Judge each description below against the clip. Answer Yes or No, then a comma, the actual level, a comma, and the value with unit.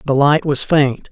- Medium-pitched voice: Yes, medium, 145 Hz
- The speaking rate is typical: No, fast, 215 wpm